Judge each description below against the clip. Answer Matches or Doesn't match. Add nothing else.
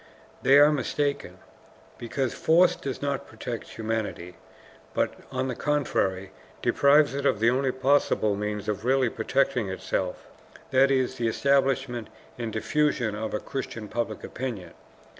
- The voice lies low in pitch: Matches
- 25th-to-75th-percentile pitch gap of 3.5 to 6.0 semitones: Matches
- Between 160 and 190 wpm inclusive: Doesn't match